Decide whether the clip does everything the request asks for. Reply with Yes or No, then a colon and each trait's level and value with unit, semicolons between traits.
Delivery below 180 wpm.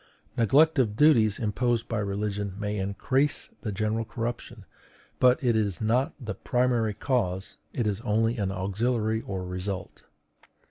Yes: average, 140 wpm